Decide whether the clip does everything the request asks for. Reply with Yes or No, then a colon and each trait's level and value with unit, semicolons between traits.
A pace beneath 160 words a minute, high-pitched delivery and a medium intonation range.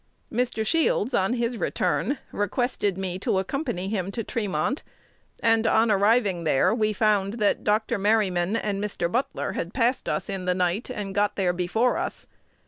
No: average, 165 wpm; high, 210 Hz; average, 3.3 semitones